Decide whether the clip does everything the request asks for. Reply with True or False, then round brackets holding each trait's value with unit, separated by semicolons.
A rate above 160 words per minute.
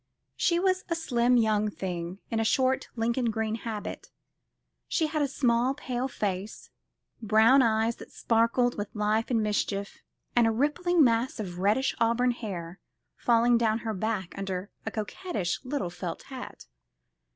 False (150 wpm)